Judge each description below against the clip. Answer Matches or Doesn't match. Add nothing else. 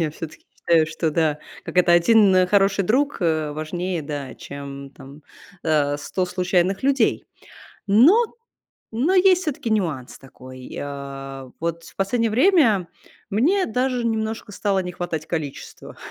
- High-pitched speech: Doesn't match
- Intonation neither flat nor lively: Doesn't match